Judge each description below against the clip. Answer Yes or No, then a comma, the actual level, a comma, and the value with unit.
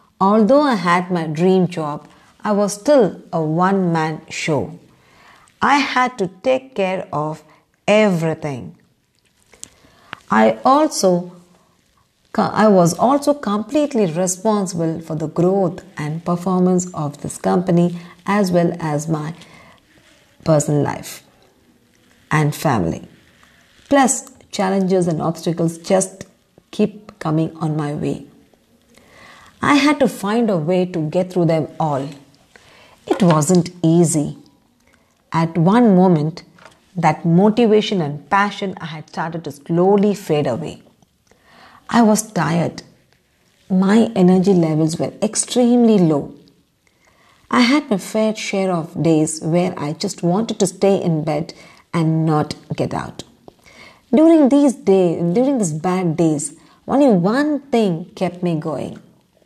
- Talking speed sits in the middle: No, slow, 120 wpm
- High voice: No, medium, 180 Hz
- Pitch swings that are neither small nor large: Yes, average, 4.4 semitones